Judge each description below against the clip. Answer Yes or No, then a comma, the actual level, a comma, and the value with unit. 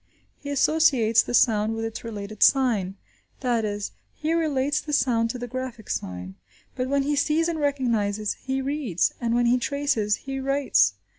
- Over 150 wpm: Yes, average, 170 wpm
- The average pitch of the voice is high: Yes, very high, 250 Hz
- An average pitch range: Yes, average, 4.5 semitones